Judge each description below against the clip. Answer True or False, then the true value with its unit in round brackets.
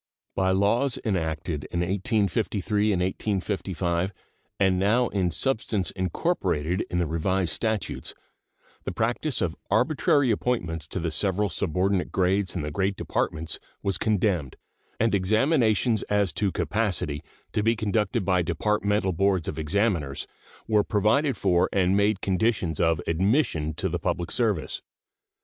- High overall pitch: False (95 Hz)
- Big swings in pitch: False (3.6 semitones)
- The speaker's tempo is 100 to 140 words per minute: True (135 wpm)